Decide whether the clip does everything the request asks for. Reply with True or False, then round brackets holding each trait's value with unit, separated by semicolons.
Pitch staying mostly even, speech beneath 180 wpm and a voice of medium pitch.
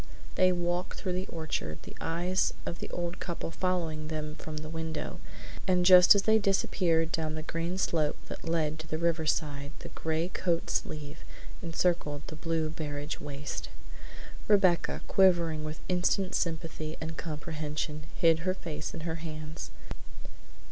True (2.3 semitones; 150 wpm; 165 Hz)